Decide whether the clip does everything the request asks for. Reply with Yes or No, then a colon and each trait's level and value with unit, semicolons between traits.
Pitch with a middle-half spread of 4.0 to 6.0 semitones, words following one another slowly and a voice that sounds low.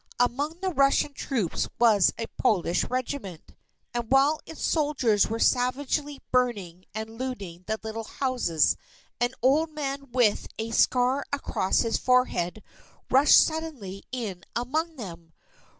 No: average, 4.6 semitones; slow, 130 wpm; high, 245 Hz